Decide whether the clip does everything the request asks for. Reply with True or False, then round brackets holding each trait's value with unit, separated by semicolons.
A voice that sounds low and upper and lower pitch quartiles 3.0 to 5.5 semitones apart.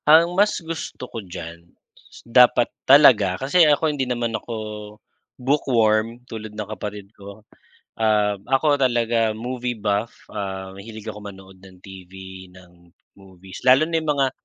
True (110 Hz; 4.6 semitones)